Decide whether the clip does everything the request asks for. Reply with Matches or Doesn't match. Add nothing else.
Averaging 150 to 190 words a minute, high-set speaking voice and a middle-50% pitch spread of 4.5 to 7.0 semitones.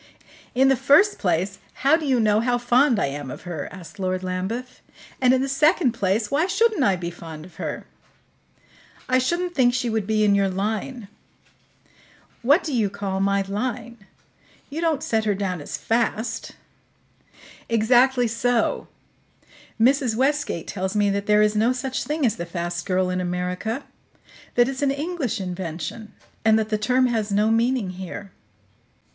Matches